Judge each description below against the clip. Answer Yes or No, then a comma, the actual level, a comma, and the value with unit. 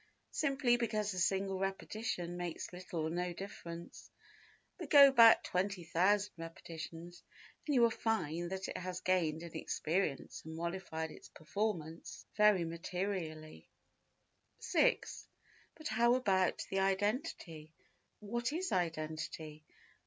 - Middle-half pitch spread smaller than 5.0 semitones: Yes, average, 4.3 semitones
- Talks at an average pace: No, slow, 120 wpm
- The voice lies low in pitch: No, medium, 185 Hz